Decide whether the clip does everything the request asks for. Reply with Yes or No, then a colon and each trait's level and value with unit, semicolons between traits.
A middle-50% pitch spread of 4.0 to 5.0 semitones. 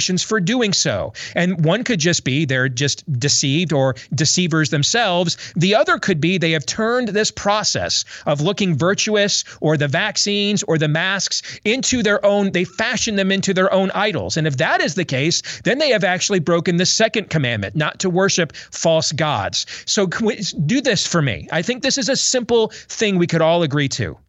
Yes: average, 4.7 semitones